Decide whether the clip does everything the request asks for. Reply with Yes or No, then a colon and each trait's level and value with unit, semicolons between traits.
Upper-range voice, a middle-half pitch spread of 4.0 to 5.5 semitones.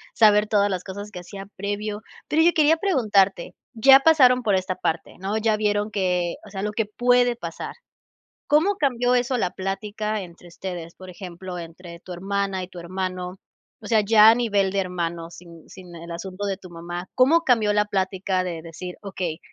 No: high, 195 Hz; average, 3.2 semitones